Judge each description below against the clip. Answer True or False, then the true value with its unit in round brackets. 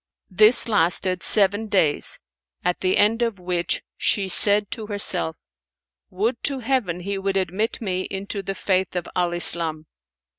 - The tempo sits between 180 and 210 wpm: False (150 wpm)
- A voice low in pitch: False (195 Hz)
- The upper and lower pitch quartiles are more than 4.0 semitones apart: False (2.8 semitones)